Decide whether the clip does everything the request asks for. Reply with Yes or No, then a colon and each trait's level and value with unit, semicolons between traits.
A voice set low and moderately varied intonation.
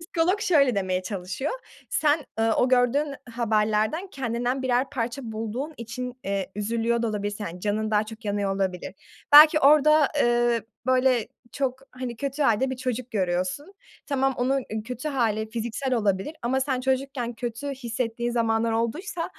No: high, 240 Hz; average, 3.7 semitones